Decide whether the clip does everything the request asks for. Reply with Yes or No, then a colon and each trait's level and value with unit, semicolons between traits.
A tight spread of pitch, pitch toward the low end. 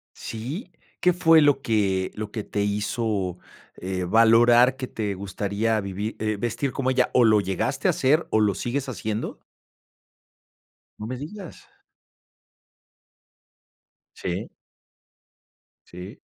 No: average, 4.2 semitones; low, 110 Hz